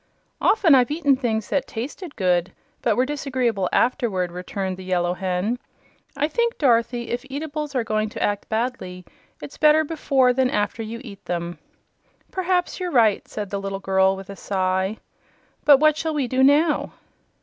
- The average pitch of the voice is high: Yes, high, 235 Hz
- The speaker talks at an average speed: Yes, average, 170 wpm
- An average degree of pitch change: No, wide, 6.7 semitones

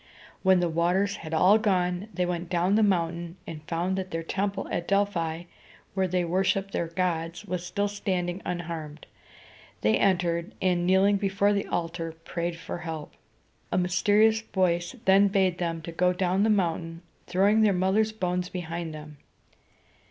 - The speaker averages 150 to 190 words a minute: Yes, average, 160 wpm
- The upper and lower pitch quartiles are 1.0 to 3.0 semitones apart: Yes, narrow, 2.5 semitones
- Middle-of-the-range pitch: Yes, medium, 180 Hz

